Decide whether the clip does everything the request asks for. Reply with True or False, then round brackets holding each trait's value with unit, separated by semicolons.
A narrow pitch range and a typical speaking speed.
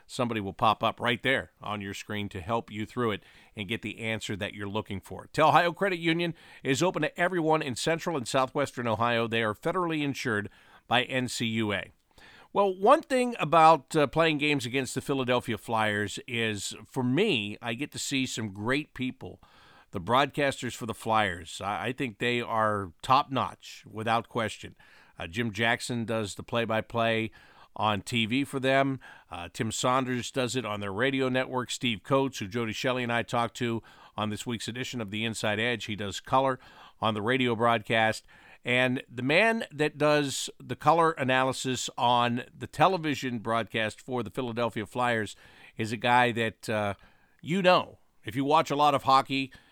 False (3.6 semitones; 180 wpm)